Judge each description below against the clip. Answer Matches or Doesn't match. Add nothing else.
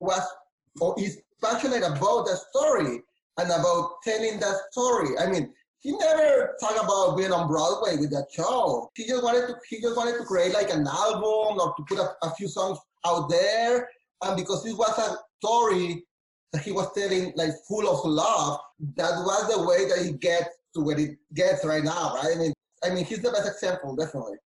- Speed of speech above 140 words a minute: Matches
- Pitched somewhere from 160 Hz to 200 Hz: Matches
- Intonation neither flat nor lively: Matches